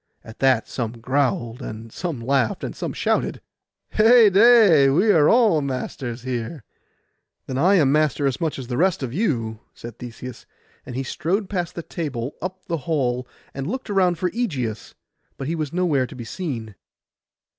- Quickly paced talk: No, average, 165 wpm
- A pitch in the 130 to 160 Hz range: Yes, medium, 140 Hz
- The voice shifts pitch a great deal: Yes, wide, 6.4 semitones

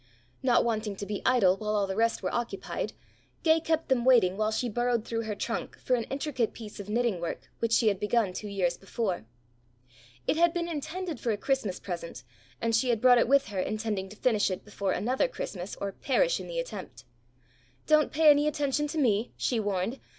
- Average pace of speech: No, fast, 210 wpm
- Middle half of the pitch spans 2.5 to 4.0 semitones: No, average, 4.9 semitones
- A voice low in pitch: No, high, 230 Hz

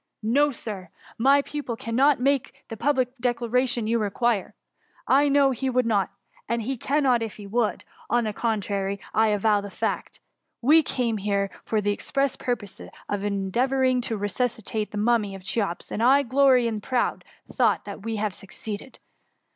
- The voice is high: Yes, high, 230 Hz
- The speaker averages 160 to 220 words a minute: Yes, average, 175 wpm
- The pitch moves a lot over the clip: No, average, 3.8 semitones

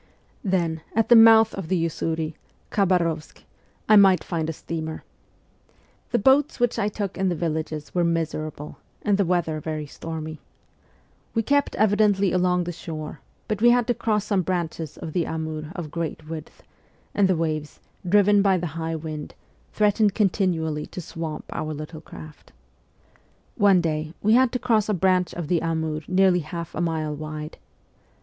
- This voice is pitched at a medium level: Yes, medium, 170 Hz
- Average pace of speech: Yes, average, 165 wpm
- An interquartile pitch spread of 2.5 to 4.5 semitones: Yes, average, 4.1 semitones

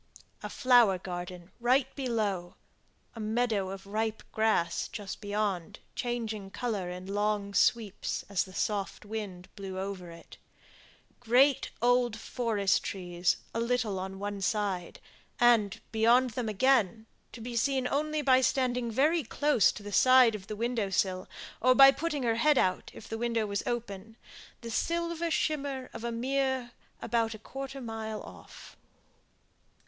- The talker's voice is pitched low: No, high, 225 Hz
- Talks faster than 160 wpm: No, average, 155 wpm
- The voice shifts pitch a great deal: No, average, 3.9 semitones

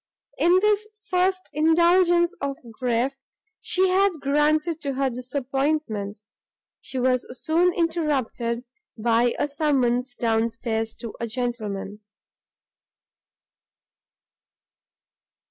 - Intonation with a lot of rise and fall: Yes, wide, 6.2 semitones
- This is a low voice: No, very high, 275 Hz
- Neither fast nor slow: No, slow, 95 wpm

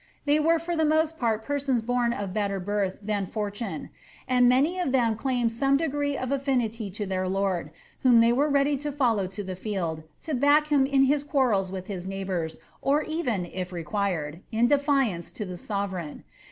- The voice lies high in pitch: Yes, high, 235 Hz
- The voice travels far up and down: Yes, wide, 6.4 semitones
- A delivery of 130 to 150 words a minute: No, average, 185 wpm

